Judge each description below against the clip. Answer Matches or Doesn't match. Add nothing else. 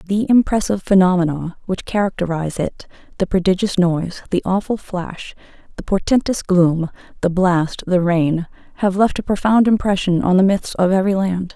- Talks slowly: Doesn't match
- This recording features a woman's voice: Matches